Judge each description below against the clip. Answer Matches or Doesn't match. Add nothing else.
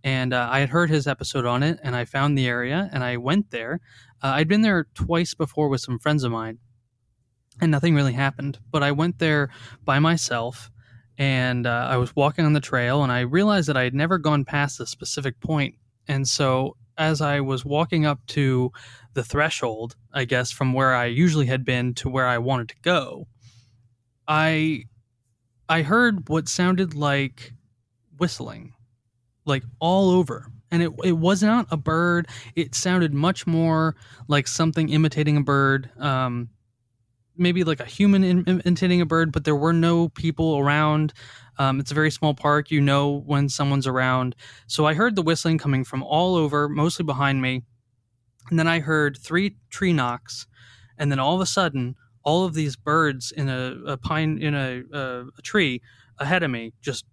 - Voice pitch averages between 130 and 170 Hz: Matches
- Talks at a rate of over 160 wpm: Matches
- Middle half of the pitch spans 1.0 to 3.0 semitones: Doesn't match